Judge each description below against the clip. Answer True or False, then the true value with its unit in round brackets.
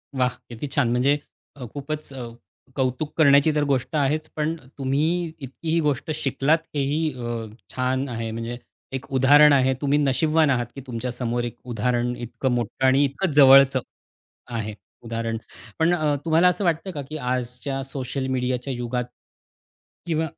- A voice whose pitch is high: False (135 Hz)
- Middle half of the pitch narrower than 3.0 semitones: False (3.3 semitones)